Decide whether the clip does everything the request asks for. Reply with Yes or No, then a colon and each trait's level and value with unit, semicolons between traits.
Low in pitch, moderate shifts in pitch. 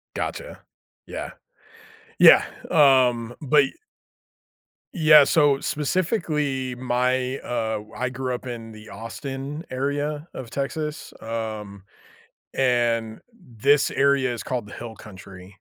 Yes: low, 130 Hz; average, 3.9 semitones